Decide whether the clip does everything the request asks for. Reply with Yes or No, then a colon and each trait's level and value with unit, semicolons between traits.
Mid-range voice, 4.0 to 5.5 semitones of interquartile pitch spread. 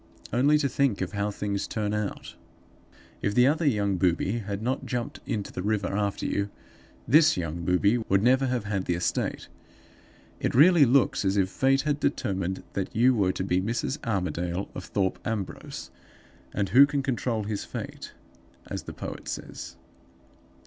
No: low, 105 Hz; average, 4.9 semitones